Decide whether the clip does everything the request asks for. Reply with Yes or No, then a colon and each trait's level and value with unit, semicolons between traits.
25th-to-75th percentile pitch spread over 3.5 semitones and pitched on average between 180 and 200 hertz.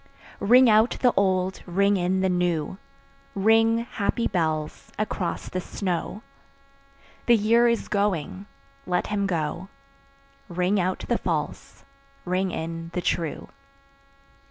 No: average, 3.1 semitones; high, 190 Hz